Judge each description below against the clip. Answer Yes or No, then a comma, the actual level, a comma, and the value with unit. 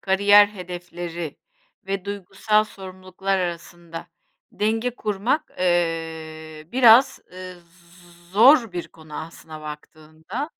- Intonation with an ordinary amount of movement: Yes, average, 3.6 semitones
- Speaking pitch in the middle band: Yes, medium, 180 Hz